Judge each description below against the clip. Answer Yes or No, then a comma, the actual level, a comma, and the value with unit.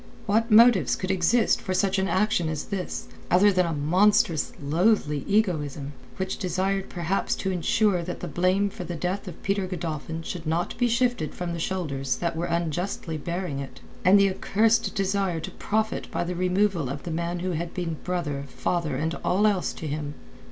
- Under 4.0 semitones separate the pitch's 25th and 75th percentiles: Yes, average, 3.3 semitones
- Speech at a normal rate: Yes, average, 190 wpm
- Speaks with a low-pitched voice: No, medium, 180 Hz